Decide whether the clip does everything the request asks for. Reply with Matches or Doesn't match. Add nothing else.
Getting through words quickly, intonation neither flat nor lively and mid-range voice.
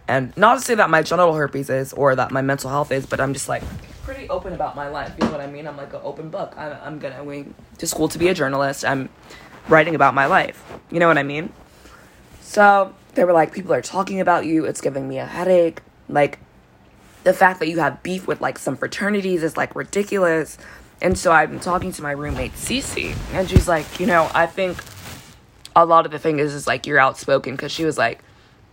Matches